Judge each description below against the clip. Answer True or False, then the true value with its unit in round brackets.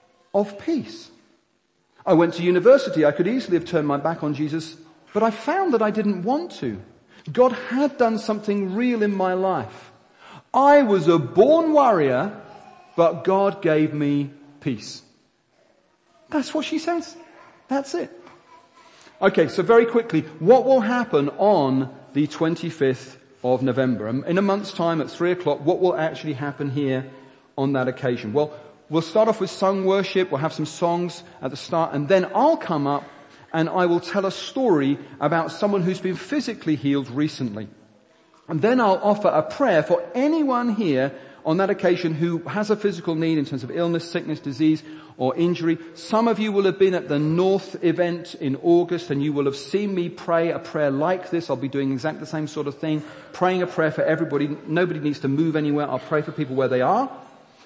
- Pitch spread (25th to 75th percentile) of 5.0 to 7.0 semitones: True (5.4 semitones)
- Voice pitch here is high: False (170 Hz)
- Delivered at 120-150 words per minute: False (185 wpm)